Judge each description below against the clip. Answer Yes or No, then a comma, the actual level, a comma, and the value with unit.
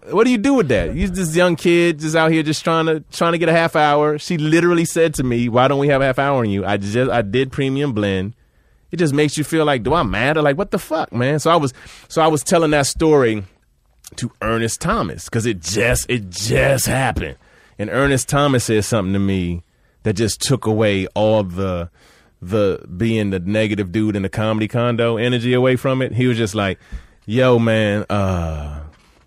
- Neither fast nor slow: No, fast, 220 wpm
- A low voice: Yes, low, 120 Hz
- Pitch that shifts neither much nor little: No, wide, 6.6 semitones